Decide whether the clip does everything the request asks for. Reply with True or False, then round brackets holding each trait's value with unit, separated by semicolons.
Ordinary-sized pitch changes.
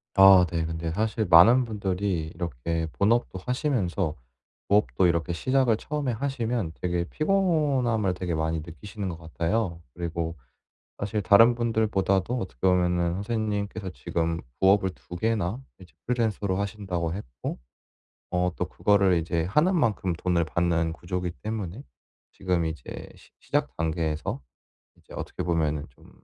True (4.6 semitones)